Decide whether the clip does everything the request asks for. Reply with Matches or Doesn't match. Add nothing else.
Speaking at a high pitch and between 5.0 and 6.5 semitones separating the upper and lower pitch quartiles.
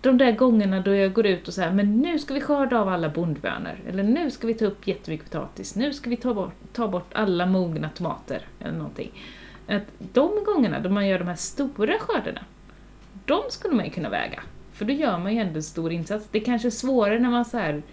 Matches